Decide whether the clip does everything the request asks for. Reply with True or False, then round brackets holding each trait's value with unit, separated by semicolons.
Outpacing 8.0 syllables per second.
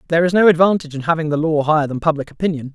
True (8.3 syllables/s)